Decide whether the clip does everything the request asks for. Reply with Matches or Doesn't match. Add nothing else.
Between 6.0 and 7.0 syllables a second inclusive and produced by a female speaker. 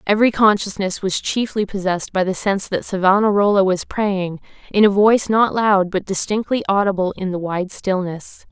Doesn't match